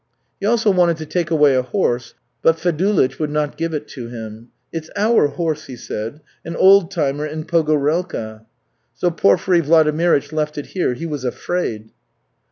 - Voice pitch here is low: No, medium, 155 Hz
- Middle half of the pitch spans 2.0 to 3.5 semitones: No, average, 3.9 semitones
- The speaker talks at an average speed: Yes, average, 170 wpm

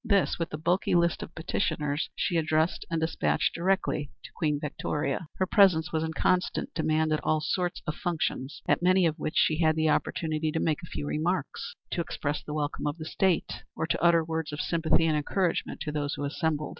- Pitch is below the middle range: No, medium, 160 Hz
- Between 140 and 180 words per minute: No, fast, 205 wpm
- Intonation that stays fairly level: Yes, narrow, 2.1 semitones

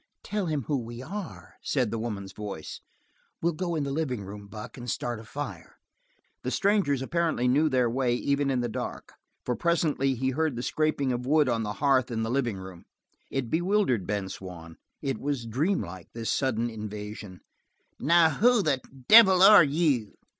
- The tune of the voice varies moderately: No, wide, 5.7 semitones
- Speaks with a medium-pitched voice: No, low, 130 Hz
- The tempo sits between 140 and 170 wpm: No, average, 180 wpm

